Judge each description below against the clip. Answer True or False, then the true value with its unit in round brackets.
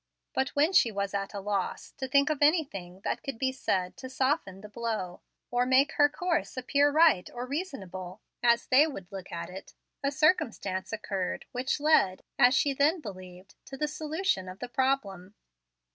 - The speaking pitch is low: False (245 Hz)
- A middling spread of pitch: False (6.9 semitones)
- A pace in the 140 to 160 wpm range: False (180 wpm)